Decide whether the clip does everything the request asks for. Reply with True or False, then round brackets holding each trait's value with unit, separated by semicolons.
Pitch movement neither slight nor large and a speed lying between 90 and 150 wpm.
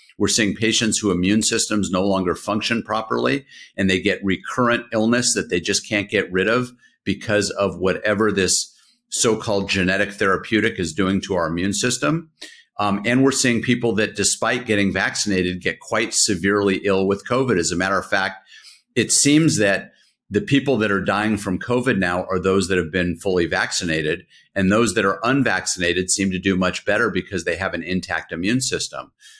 False (3.3 semitones; 185 wpm)